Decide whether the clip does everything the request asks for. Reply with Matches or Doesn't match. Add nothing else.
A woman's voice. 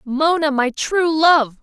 Matches